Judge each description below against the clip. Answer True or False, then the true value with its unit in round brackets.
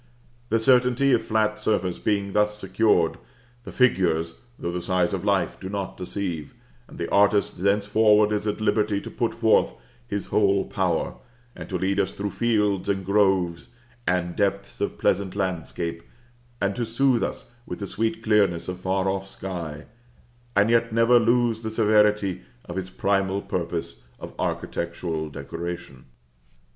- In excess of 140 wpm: True (155 wpm)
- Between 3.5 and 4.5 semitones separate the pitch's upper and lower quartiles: False (2.9 semitones)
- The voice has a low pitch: True (100 Hz)